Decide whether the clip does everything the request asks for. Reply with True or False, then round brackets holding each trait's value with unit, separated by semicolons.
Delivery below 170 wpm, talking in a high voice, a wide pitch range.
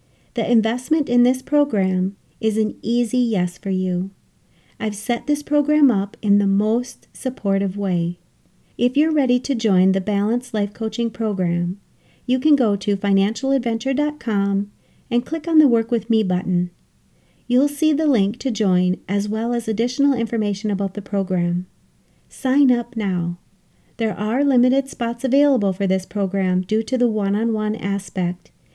False (160 wpm; 220 Hz; 4.1 semitones)